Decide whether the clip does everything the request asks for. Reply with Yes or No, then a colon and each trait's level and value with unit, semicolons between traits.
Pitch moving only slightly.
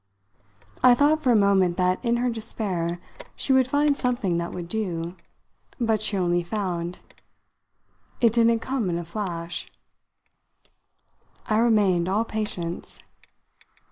No: average, 5.1 semitones